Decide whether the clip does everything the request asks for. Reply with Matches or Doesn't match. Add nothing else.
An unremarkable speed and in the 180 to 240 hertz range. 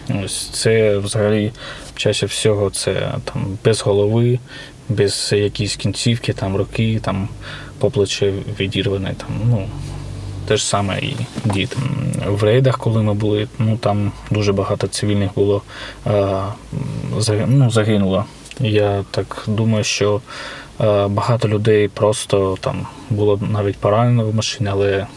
Doesn't match